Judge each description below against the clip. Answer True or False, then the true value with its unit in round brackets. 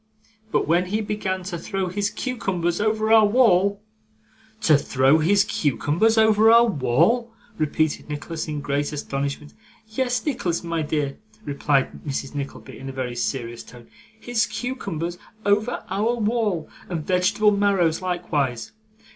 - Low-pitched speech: False (180 Hz)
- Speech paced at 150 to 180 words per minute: False (140 wpm)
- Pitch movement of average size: False (6.4 semitones)